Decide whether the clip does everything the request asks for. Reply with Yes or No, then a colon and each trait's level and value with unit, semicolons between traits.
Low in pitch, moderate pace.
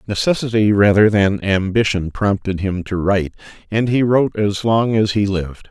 Yes: low, 105 Hz; average, 170 wpm